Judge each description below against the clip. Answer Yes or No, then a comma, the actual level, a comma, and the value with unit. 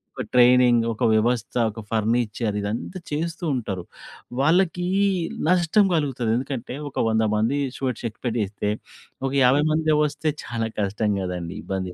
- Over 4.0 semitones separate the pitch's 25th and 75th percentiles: Yes, average, 5.1 semitones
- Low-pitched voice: Yes, low, 120 Hz